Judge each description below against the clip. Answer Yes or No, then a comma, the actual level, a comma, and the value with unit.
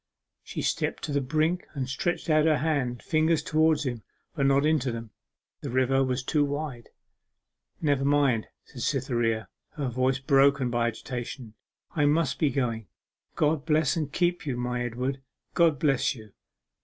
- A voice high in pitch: No, low, 135 Hz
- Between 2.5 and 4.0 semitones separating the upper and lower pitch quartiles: Yes, average, 3.7 semitones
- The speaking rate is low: No, average, 165 wpm